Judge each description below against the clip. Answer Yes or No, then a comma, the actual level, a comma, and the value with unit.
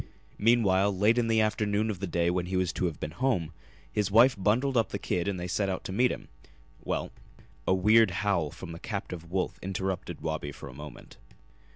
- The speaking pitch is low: Yes, very low, 95 Hz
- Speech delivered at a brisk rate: Yes, fast, 215 wpm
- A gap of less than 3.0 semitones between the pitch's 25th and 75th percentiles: No, average, 3.6 semitones